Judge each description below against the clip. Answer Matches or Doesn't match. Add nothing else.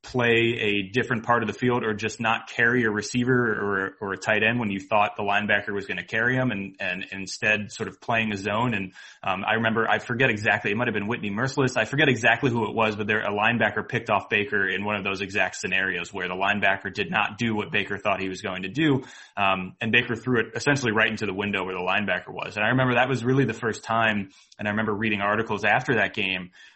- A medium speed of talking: Doesn't match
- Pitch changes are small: Doesn't match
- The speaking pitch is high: Doesn't match